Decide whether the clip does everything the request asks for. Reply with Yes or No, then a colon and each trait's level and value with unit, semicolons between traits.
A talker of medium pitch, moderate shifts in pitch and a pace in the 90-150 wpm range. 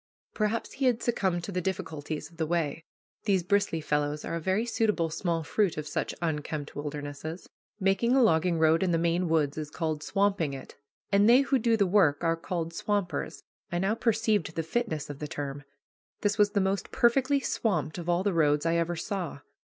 No: medium, 175 Hz; average, 4.6 semitones; average, 195 wpm